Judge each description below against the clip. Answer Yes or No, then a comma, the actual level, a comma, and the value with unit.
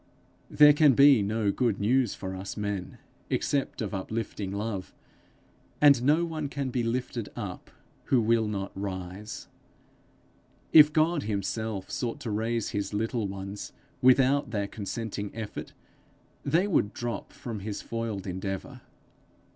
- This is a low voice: Yes, low, 110 Hz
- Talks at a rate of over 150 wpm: No, slow, 135 wpm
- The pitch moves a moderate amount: Yes, average, 4.3 semitones